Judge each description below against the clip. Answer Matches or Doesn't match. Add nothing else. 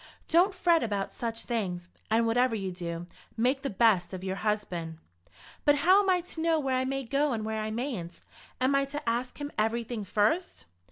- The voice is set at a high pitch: Matches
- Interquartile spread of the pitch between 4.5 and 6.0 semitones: Matches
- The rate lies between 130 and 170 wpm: Doesn't match